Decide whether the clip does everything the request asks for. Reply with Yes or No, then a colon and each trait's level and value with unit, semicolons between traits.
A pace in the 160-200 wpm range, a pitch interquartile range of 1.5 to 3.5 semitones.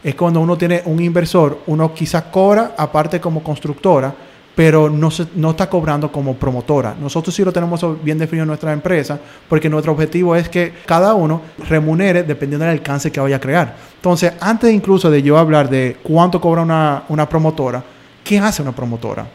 Yes: average, 185 wpm; average, 2.7 semitones